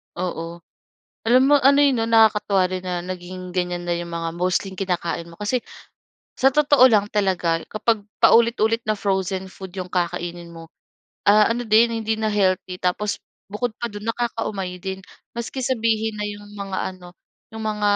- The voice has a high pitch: Yes, high, 205 Hz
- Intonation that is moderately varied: Yes, average, 3.7 semitones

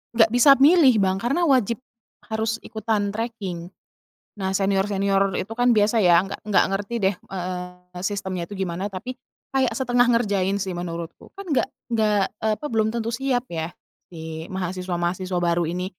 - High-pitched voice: Yes, high, 200 Hz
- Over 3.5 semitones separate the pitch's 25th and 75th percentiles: Yes, average, 4.0 semitones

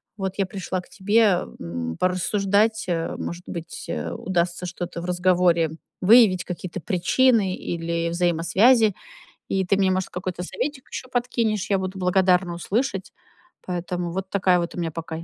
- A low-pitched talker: No, medium, 185 Hz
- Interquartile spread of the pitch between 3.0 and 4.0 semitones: No, narrow, 2.4 semitones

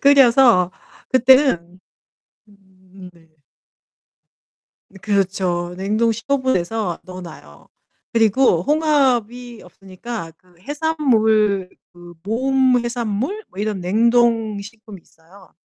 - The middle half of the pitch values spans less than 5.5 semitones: Yes, average, 5.1 semitones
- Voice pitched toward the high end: Yes, high, 215 Hz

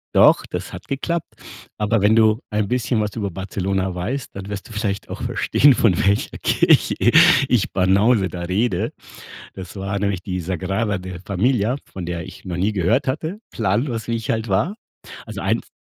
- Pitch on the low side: Yes, low, 100 Hz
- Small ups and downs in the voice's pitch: No, average, 3.4 semitones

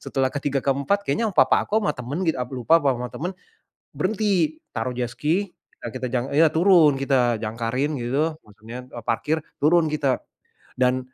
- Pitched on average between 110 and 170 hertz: Yes, medium, 140 Hz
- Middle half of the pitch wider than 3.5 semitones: Yes, average, 4.6 semitones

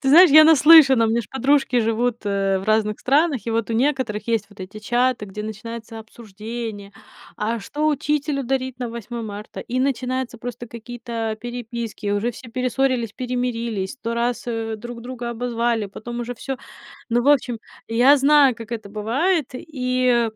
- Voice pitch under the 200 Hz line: No, high, 235 Hz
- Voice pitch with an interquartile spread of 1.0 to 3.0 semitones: Yes, narrow, 2.6 semitones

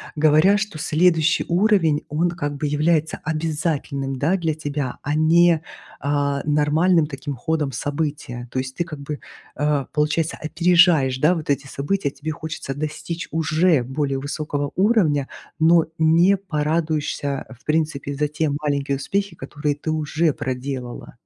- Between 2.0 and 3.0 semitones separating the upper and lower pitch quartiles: Yes, narrow, 2.5 semitones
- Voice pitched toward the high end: No, medium, 150 Hz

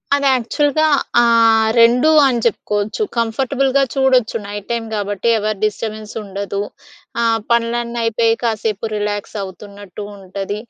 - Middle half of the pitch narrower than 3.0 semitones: Yes, narrow, 2.4 semitones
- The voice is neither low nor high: No, high, 225 Hz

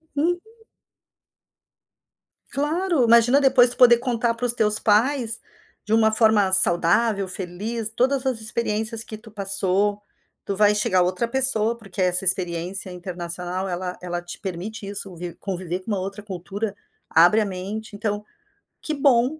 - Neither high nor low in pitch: No, high, 210 Hz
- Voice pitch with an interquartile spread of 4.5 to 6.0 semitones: No, average, 4.0 semitones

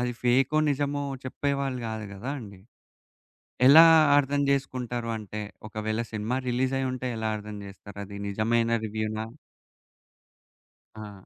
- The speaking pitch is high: No, low, 115 Hz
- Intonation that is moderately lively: Yes, average, 3.6 semitones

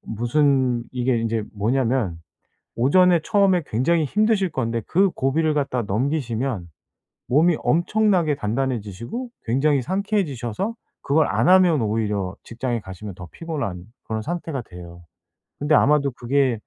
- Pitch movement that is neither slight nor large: No, wide, 6.3 semitones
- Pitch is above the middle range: No, low, 135 Hz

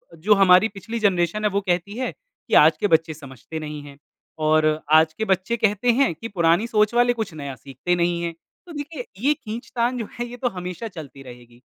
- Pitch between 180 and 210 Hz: Yes, high, 190 Hz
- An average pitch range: No, wide, 6.4 semitones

